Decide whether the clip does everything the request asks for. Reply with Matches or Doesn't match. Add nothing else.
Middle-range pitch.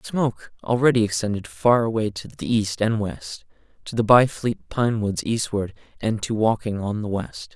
Doesn't match